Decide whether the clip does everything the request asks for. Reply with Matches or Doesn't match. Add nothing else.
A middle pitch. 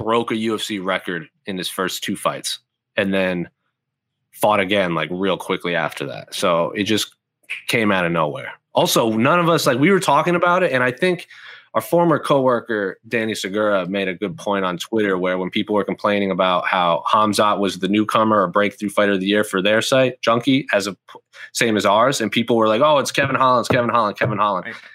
Doesn't match